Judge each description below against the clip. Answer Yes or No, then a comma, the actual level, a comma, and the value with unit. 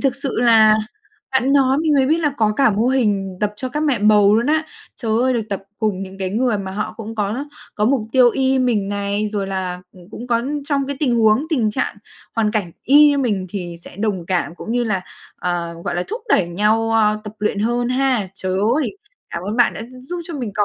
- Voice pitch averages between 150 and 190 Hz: No, high, 220 Hz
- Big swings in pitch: No, average, 4.6 semitones